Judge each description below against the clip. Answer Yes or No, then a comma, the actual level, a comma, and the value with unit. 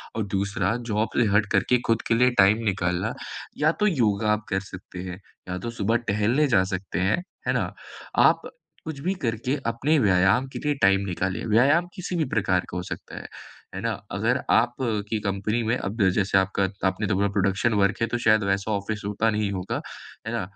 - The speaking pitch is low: Yes, low, 105 Hz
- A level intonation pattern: No, average, 3.2 semitones